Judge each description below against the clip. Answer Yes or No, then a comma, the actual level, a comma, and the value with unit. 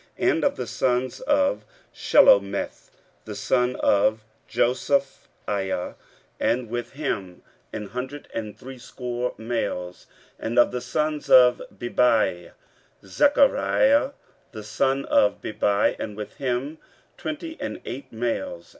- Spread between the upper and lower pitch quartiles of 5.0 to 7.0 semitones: No, average, 4.3 semitones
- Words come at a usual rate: No, slow, 120 wpm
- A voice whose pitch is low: Yes, low, 125 Hz